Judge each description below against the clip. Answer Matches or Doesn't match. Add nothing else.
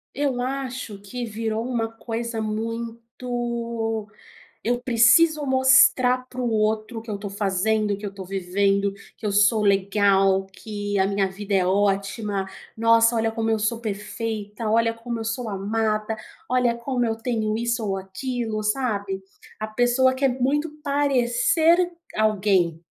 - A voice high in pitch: Matches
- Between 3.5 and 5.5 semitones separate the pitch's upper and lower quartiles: Doesn't match